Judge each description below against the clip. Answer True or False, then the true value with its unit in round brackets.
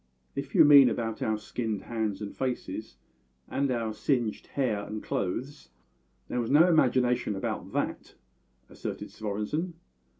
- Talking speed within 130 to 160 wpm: True (135 wpm)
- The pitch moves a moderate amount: True (4.3 semitones)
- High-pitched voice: False (120 Hz)